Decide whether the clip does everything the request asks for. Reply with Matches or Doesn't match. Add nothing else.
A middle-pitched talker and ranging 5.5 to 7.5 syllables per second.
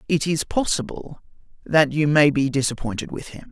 Doesn't match